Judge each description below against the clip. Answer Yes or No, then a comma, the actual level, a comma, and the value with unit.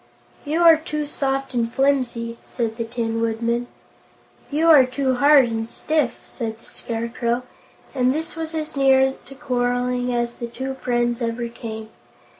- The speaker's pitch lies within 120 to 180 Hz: No, very high, 250 Hz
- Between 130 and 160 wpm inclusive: Yes, average, 155 wpm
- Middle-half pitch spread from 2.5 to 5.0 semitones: Yes, average, 2.9 semitones